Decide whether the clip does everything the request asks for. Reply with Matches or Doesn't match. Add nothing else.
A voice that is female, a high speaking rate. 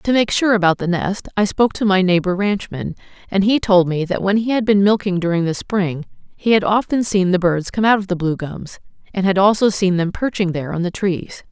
Matches